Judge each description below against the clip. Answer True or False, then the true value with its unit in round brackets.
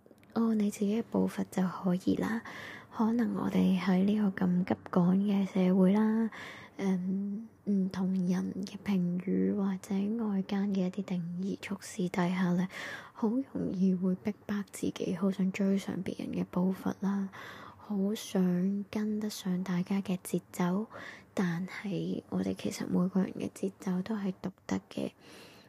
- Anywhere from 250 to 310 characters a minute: False (215 characters per minute)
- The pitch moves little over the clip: True (2.1 semitones)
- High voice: True (195 Hz)